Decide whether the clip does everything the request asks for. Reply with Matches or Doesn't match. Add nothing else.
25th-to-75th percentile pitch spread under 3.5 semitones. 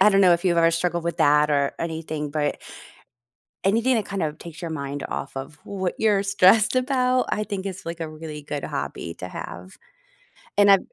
Doesn't match